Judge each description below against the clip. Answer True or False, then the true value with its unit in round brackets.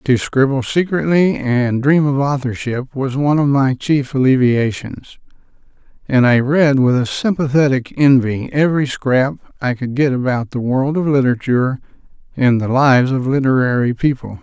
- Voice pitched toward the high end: False (135 Hz)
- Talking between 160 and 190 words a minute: False (150 wpm)